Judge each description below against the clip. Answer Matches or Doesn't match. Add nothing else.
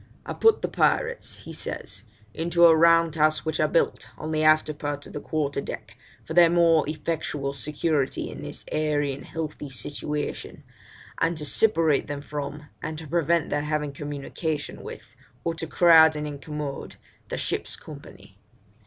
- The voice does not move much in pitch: Matches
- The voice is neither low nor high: Matches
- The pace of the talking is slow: Doesn't match